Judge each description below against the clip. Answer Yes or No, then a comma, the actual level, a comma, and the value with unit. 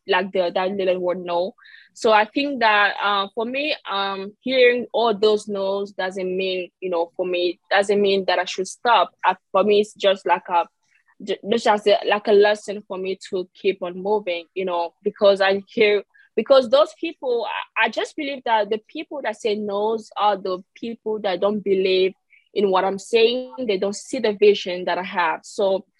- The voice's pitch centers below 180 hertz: No, high, 200 Hz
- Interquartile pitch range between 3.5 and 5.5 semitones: No, average, 2.8 semitones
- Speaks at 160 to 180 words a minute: No, average, 190 wpm